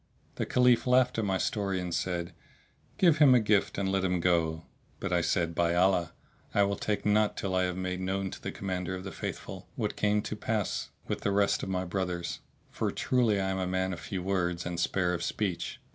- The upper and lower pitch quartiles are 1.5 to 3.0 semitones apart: Yes, narrow, 2.5 semitones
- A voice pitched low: Yes, very low, 95 Hz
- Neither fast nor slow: No, fast, 220 wpm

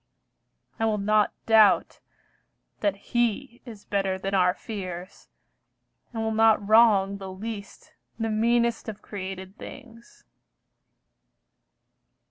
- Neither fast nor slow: No, slow, 105 wpm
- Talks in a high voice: Yes, high, 210 Hz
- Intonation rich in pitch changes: No, narrow, 2.5 semitones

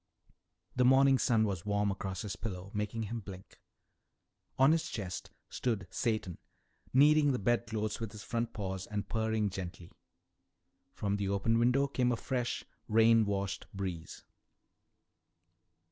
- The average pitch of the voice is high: No, low, 110 Hz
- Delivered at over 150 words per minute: No, slow, 135 wpm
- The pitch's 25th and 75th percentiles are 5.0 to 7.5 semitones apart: No, average, 3.4 semitones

